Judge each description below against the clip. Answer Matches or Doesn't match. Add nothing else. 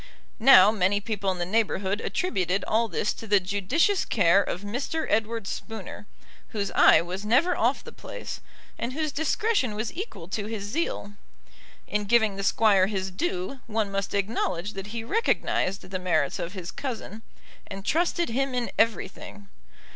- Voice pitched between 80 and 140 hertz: Doesn't match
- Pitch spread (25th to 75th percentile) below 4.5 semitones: Matches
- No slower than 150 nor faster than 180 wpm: Matches